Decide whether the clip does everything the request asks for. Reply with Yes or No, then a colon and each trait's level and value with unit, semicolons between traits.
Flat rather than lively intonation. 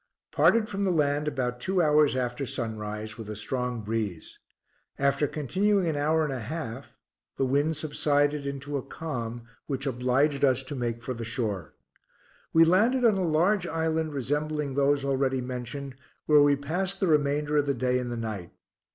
No: average, 3.8 semitones